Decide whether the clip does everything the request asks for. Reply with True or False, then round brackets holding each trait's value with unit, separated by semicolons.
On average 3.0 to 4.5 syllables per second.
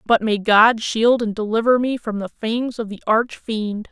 True (4.3 syllables/s)